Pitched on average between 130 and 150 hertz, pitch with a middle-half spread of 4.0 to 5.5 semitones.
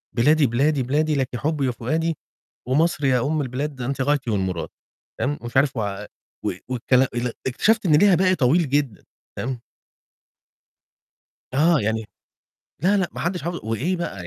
Yes: medium, 140 Hz; average, 4.5 semitones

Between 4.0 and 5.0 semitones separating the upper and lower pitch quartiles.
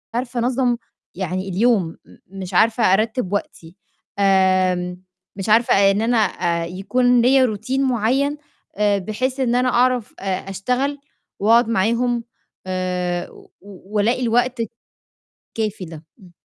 Yes: average, 4.7 semitones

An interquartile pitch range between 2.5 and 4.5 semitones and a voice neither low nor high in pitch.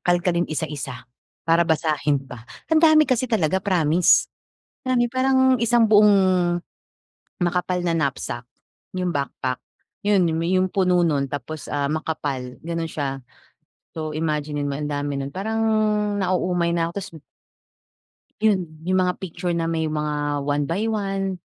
Yes: average, 4.2 semitones; medium, 170 Hz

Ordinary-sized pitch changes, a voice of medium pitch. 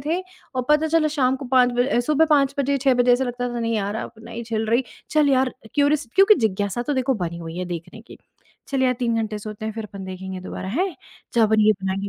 No: average, 4.5 semitones; high, 245 Hz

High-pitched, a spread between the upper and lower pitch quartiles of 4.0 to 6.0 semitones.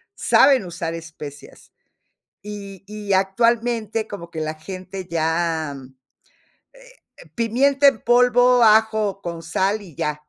Yes: high, 195 Hz; wide, 5.6 semitones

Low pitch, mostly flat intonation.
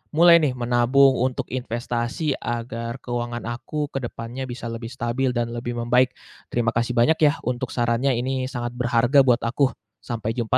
Yes: low, 120 Hz; narrow, 1.7 semitones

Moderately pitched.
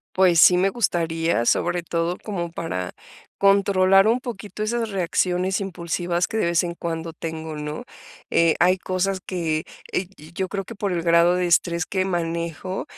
Yes: medium, 175 Hz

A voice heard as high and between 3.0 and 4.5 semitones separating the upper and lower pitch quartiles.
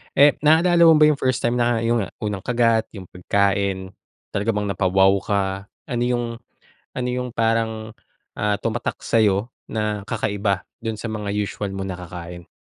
No: low, 110 Hz; average, 3.3 semitones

